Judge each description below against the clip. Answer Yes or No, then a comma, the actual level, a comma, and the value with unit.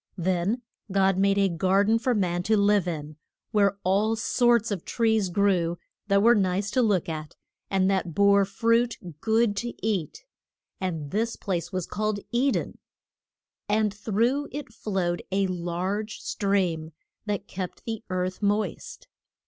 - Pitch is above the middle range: Yes, high, 200 Hz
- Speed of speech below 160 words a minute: Yes, average, 150 wpm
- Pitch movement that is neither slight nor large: Yes, average, 3.2 semitones